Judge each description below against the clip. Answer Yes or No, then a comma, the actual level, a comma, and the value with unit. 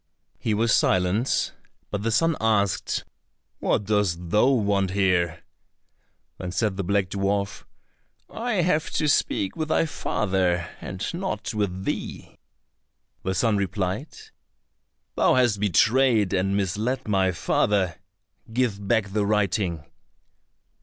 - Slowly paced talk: Yes, slow, 120 wpm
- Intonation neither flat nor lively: Yes, average, 3.2 semitones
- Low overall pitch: Yes, low, 100 Hz